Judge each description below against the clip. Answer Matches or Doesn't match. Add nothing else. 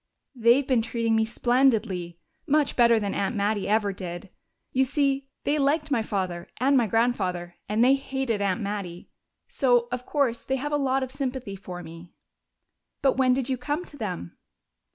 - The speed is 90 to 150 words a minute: Doesn't match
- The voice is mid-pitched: Doesn't match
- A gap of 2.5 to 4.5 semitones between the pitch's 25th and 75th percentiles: Doesn't match